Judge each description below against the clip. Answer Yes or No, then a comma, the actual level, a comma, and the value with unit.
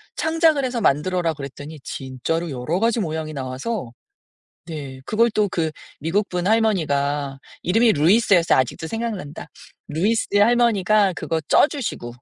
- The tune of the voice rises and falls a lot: Yes, wide, 7.3 semitones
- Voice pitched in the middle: Yes, medium, 175 Hz